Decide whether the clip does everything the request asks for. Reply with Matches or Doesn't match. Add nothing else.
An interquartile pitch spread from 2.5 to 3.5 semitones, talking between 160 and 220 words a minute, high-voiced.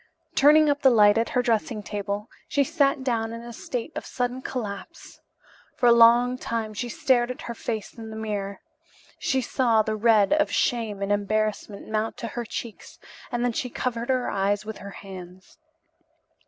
Matches